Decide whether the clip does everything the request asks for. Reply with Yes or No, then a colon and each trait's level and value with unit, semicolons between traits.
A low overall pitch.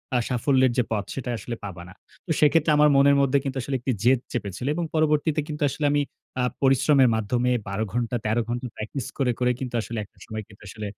Yes: low, 125 Hz